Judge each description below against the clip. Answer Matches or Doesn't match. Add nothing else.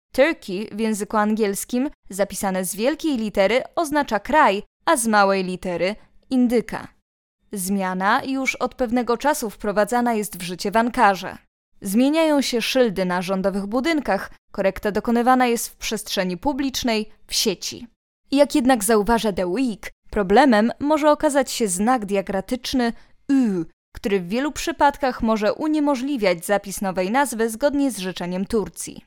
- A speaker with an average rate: Matches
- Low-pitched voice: Doesn't match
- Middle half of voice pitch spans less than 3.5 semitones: Doesn't match